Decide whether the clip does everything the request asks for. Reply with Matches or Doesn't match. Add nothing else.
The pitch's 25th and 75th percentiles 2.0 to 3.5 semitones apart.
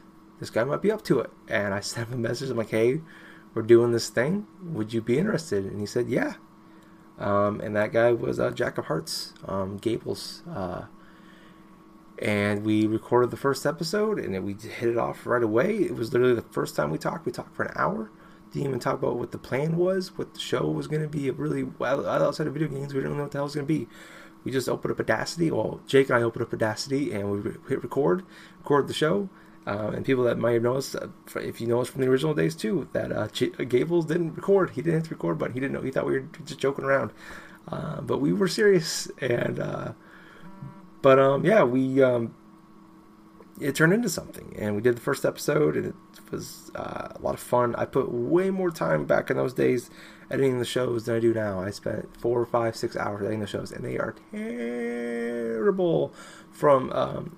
Doesn't match